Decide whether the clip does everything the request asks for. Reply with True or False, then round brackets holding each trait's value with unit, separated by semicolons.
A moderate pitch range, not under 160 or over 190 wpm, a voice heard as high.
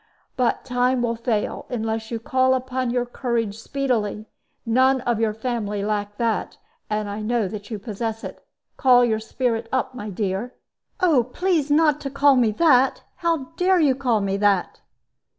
True (3.3 semitones; 170 wpm; 240 Hz)